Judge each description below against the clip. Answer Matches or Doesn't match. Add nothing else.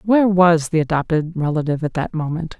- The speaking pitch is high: Doesn't match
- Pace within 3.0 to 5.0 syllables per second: Doesn't match